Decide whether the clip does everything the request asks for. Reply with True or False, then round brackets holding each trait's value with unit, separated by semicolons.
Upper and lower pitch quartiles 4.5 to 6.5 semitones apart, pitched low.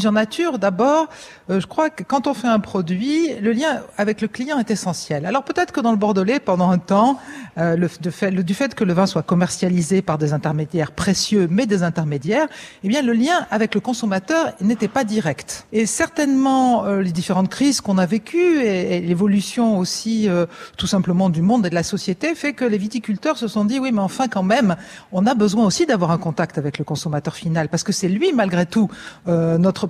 False (5.2 semitones; 205 Hz)